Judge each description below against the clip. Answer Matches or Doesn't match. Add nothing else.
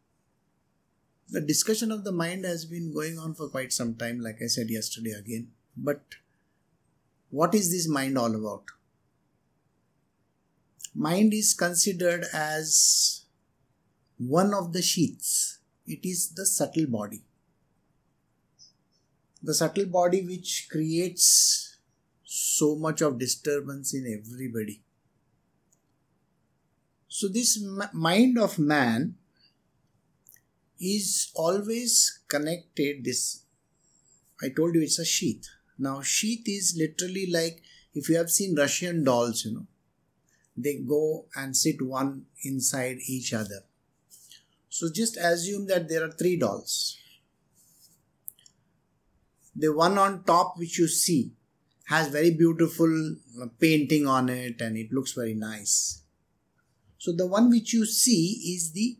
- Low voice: Doesn't match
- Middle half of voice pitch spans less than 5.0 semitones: Doesn't match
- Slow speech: Matches